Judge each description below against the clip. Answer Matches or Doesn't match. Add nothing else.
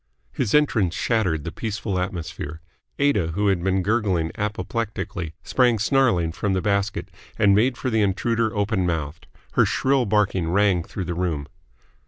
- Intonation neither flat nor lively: Matches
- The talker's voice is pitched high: Doesn't match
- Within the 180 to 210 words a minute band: Doesn't match